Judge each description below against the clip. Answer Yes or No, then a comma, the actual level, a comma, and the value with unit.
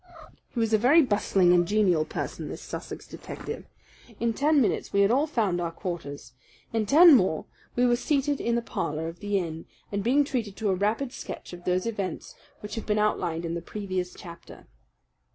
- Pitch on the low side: No, high, 205 Hz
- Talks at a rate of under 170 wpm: No, average, 195 wpm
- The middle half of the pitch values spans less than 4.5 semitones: No, average, 5.1 semitones